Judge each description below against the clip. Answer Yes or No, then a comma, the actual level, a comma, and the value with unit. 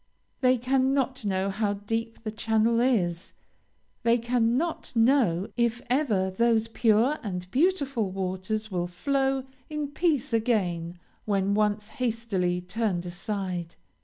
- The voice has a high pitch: Yes, high, 225 Hz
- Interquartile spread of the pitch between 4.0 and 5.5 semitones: Yes, average, 4.8 semitones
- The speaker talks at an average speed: No, slow, 120 wpm